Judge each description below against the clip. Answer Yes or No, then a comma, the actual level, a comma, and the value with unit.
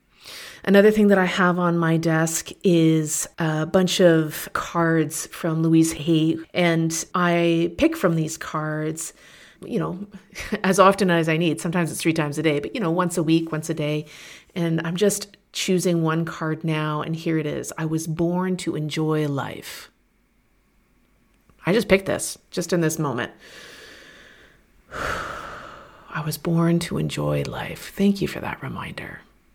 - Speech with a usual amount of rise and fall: No, narrow, 2.2 semitones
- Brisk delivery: No, average, 160 wpm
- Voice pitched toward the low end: No, medium, 165 Hz